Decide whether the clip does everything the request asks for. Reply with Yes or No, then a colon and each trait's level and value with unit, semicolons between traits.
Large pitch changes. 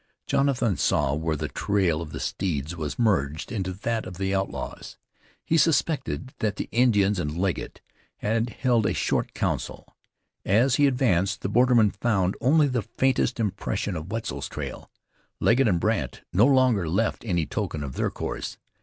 Yes: wide, 5.7 semitones